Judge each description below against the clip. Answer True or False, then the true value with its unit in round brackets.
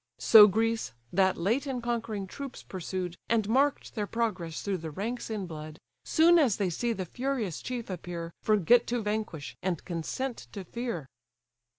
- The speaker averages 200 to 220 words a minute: False (165 wpm)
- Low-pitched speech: False (210 Hz)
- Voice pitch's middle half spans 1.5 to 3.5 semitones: False (4.9 semitones)